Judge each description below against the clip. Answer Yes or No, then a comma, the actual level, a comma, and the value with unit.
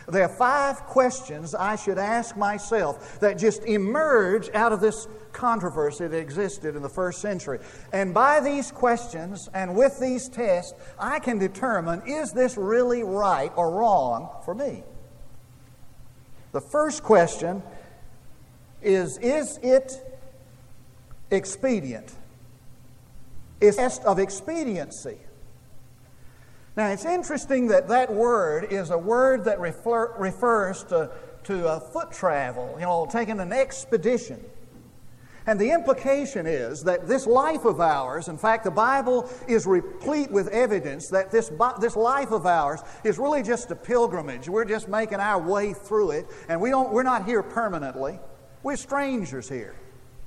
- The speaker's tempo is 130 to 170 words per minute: Yes, average, 140 wpm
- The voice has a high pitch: Yes, high, 215 Hz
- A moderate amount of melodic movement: No, wide, 6.2 semitones